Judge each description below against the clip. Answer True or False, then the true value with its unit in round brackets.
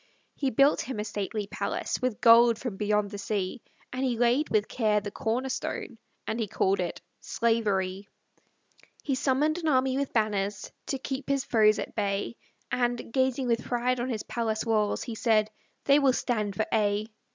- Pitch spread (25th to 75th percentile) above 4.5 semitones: False (3.5 semitones)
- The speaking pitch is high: True (230 Hz)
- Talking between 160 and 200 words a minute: True (180 wpm)